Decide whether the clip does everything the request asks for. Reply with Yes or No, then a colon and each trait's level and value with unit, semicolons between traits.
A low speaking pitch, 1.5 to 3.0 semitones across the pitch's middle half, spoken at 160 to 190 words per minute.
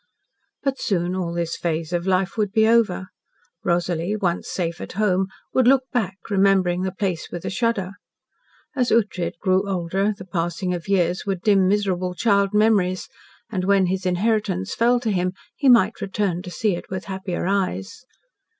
No: high, 190 Hz; average, 2.7 semitones; average, 170 wpm